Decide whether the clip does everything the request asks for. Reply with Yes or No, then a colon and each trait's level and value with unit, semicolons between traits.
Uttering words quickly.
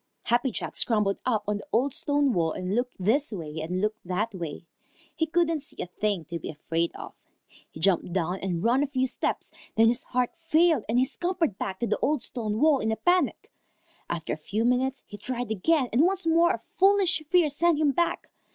Yes: fast, 215 wpm